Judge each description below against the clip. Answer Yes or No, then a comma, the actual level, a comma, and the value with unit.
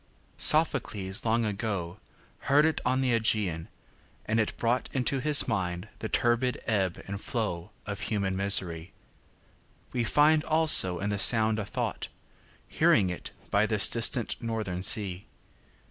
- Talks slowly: Yes, slow, 120 wpm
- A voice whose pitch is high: No, low, 110 Hz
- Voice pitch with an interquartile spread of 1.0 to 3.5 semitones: No, average, 4.0 semitones